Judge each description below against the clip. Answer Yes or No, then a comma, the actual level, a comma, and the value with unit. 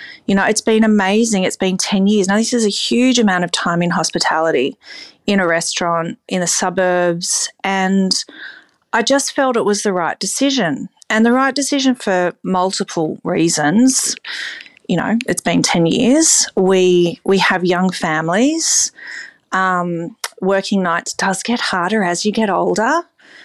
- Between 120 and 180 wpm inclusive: Yes, average, 160 wpm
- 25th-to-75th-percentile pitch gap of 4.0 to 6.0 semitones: Yes, average, 4.6 semitones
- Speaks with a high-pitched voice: Yes, high, 195 Hz